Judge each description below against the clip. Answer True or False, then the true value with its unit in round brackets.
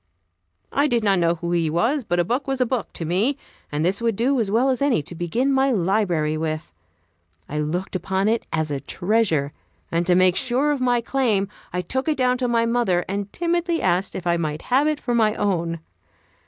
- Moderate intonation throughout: False (6.6 semitones)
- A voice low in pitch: False (205 Hz)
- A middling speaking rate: False (220 wpm)